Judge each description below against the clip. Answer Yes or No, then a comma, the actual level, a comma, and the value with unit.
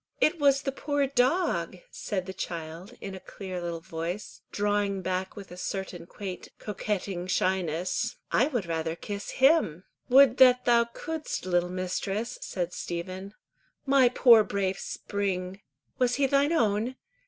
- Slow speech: No, average, 145 wpm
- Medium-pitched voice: No, high, 200 Hz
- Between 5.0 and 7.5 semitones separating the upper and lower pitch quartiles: Yes, wide, 5.5 semitones